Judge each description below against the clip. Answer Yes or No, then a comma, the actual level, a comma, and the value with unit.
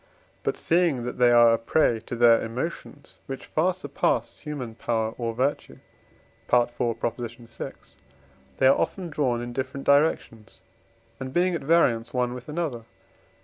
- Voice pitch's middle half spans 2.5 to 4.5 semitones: Yes, average, 4.1 semitones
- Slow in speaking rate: No, average, 150 wpm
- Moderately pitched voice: No, low, 125 Hz